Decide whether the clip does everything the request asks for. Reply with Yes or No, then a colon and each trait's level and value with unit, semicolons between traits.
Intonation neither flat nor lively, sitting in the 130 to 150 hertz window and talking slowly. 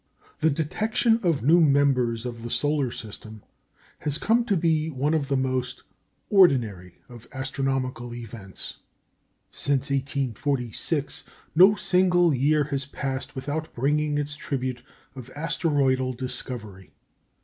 Yes: average, 3.4 semitones; medium, 140 Hz; slow, 120 wpm